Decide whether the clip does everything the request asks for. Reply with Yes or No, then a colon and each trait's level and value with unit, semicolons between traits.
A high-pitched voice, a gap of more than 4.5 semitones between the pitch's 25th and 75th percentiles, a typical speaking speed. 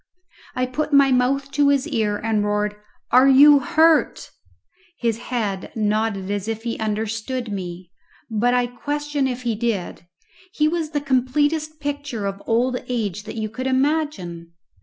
Yes: high, 245 Hz; average, 5.0 semitones; average, 155 wpm